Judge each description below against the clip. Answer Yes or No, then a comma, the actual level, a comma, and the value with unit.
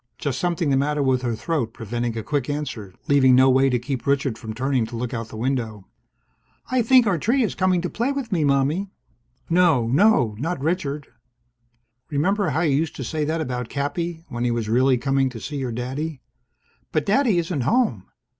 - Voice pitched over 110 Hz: Yes, medium, 140 Hz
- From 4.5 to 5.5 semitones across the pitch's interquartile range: Yes, average, 5.2 semitones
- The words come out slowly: No, average, 200 wpm